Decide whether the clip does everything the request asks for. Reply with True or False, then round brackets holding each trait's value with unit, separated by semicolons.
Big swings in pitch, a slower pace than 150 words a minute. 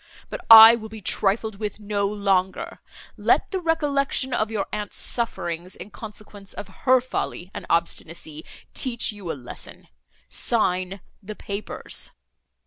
False (3.7 semitones; 135 wpm)